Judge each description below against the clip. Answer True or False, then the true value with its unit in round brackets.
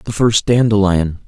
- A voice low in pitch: True (105 Hz)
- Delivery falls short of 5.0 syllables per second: True (4.2 syllables/s)